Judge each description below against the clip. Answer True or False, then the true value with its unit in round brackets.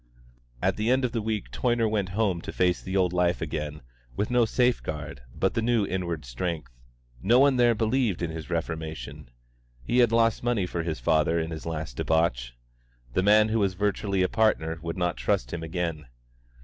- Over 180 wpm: True (195 wpm)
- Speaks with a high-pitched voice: False (90 Hz)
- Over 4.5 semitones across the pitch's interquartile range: True (5.5 semitones)